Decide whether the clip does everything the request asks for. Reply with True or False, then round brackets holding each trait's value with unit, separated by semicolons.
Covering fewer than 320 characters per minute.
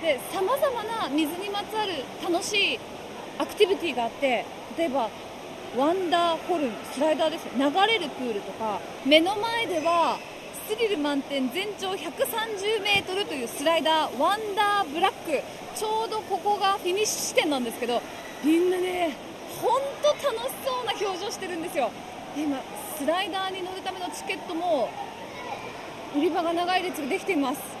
False (330 characters per minute)